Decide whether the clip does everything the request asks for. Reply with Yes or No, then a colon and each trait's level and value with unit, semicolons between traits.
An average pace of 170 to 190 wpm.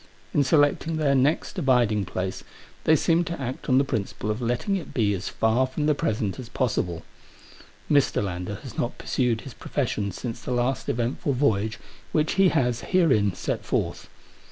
Yes: average, 175 wpm